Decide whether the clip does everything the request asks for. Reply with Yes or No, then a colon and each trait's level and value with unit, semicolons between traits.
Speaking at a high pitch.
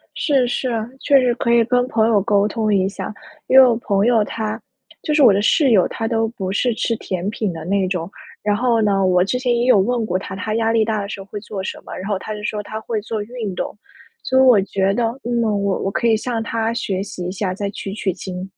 Yes: high, 215 Hz